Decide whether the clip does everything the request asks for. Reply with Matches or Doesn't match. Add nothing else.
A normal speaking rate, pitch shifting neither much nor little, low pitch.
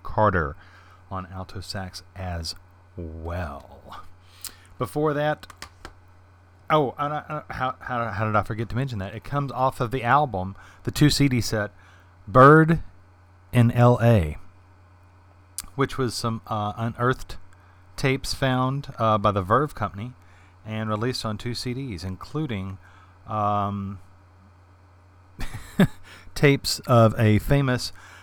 Doesn't match